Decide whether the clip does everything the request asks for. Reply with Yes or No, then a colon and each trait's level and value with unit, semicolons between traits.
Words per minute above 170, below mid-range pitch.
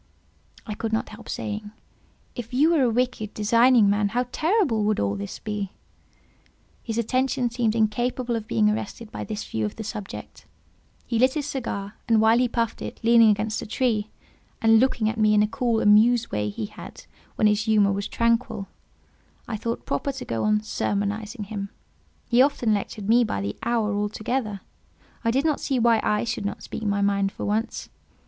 No: average, 185 wpm; high, 220 Hz